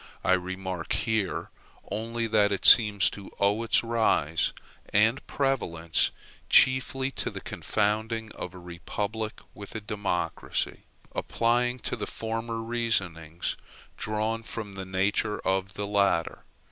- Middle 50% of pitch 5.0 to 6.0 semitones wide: No, average, 3.2 semitones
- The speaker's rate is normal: No, slow, 125 wpm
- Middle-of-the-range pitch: No, low, 105 Hz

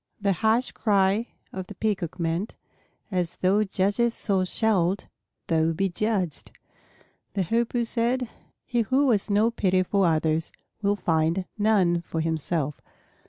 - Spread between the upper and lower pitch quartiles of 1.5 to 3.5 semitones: No, average, 4.2 semitones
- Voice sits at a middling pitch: No, high, 195 Hz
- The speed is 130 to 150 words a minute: Yes, slow, 135 wpm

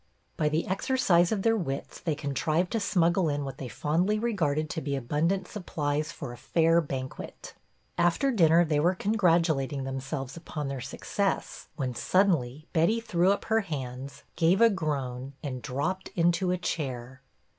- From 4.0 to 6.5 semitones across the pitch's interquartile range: Yes, average, 5.0 semitones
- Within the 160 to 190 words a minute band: Yes, average, 170 wpm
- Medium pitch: Yes, medium, 160 Hz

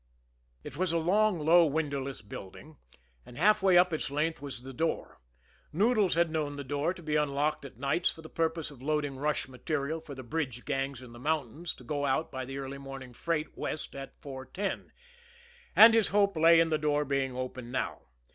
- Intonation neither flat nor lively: Yes, average, 3.4 semitones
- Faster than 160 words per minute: Yes, average, 195 wpm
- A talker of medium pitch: Yes, medium, 150 Hz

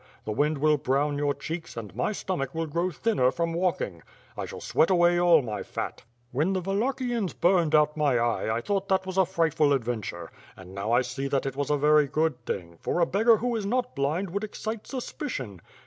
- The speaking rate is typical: No, fast, 210 wpm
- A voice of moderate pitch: Yes, medium, 155 Hz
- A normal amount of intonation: No, wide, 6.1 semitones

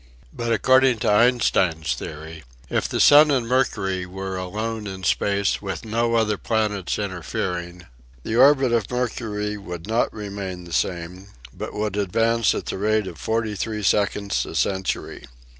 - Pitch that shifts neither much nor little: Yes, average, 3.5 semitones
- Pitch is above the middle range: No, low, 105 Hz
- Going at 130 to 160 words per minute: Yes, average, 150 wpm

